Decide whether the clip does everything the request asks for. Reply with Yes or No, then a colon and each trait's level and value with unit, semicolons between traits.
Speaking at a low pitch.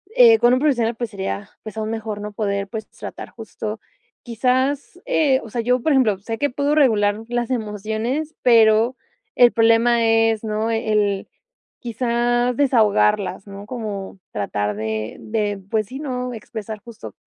No: high, 225 Hz